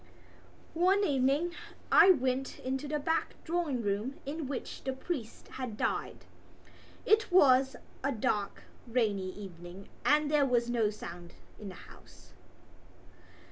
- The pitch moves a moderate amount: No, wide, 5.9 semitones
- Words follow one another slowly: Yes, slow, 130 wpm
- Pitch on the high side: Yes, very high, 260 Hz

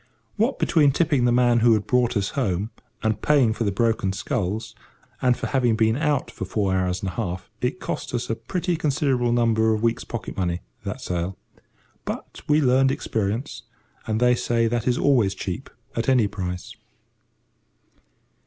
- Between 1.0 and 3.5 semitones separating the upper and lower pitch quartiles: No, average, 4.2 semitones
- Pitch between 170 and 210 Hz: No, low, 115 Hz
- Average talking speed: Yes, average, 170 wpm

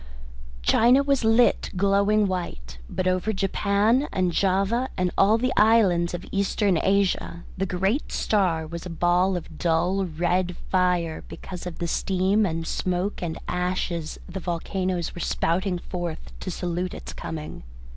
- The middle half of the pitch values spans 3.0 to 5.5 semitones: No, narrow, 2.5 semitones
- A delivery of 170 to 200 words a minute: No, average, 145 wpm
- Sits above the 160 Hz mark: Yes, medium, 185 Hz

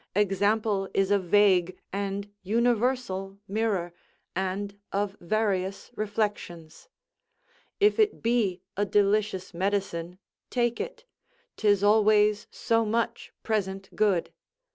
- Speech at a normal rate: No, slow, 100 wpm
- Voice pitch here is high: Yes, high, 205 Hz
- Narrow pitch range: Yes, narrow, 2.1 semitones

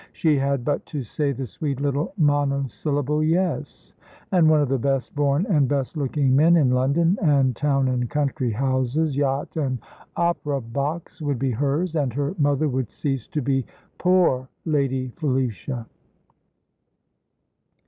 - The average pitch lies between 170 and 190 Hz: No, medium, 140 Hz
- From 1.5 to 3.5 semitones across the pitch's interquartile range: Yes, narrow, 2.5 semitones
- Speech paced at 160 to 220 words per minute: No, average, 150 wpm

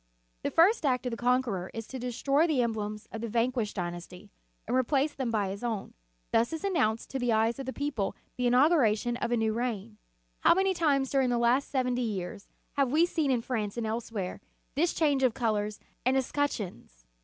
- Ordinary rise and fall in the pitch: Yes, average, 3.8 semitones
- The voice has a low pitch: No, high, 240 Hz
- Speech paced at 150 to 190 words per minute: No, fast, 205 wpm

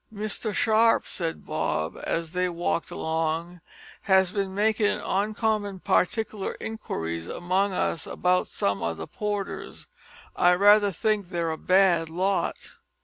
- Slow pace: Yes, slow, 130 wpm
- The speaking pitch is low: No, medium, 185 Hz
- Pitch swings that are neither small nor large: Yes, average, 3.7 semitones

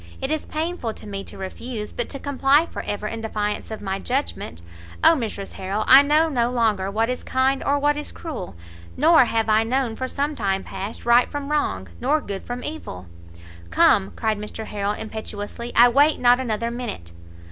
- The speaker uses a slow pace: No, average, 190 wpm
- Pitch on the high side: Yes, high, 235 Hz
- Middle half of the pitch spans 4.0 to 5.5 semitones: Yes, average, 5.0 semitones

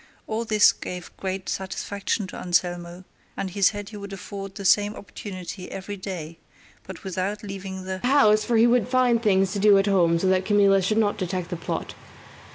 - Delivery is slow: No, average, 190 wpm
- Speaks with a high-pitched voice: Yes, high, 195 Hz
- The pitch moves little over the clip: Yes, narrow, 2.1 semitones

